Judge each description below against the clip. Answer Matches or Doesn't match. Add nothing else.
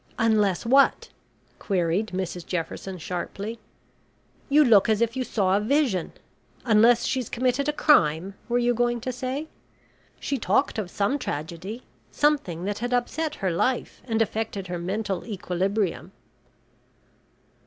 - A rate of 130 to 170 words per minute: Matches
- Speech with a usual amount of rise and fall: Matches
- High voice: Matches